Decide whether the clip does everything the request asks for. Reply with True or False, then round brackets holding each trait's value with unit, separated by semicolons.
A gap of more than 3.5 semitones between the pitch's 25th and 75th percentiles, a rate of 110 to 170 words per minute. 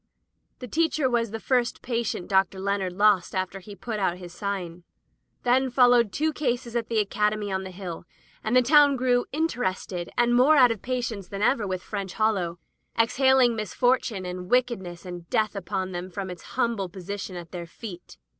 False (4.7 semitones; 180 wpm)